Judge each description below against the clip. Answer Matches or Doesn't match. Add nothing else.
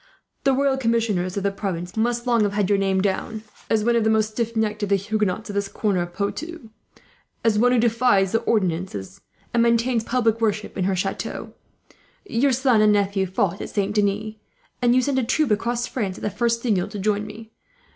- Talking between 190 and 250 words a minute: Matches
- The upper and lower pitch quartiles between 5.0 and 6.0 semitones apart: Doesn't match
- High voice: Matches